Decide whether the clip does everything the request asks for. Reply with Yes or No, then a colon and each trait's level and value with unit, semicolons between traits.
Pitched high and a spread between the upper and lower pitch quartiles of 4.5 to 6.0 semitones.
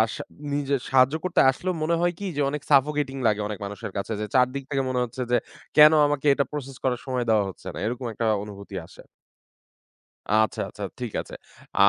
No: low, 130 Hz; average, 4.9 semitones